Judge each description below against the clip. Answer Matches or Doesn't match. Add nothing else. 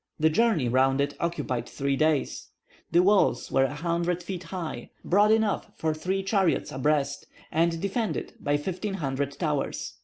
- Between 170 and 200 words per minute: Doesn't match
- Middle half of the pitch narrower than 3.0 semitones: Doesn't match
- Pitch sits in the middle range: Matches